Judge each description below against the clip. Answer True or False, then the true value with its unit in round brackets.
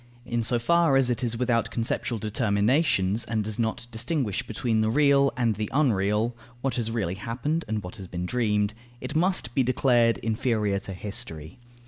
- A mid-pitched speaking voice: False (115 Hz)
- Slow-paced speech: False (175 wpm)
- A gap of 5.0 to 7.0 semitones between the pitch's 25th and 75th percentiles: False (3.2 semitones)